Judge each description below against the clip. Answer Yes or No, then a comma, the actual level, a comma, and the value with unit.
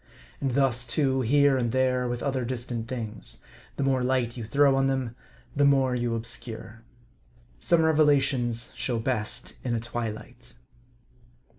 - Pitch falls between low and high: No, low, 125 Hz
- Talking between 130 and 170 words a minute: Yes, average, 145 wpm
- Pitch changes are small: Yes, narrow, 2.3 semitones